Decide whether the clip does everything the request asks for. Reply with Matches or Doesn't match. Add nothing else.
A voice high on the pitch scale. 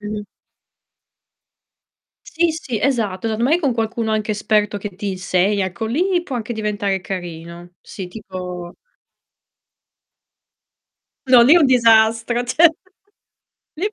Matches